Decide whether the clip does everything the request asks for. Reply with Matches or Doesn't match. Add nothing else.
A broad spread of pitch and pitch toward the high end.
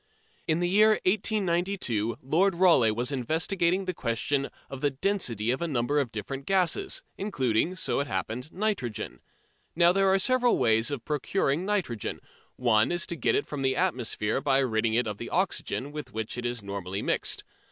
Doesn't match